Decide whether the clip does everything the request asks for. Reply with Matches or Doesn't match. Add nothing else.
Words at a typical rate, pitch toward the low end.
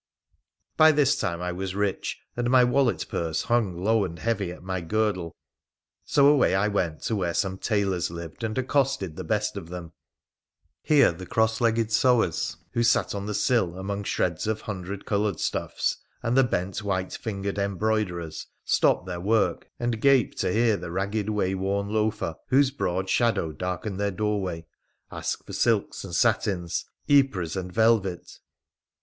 Matches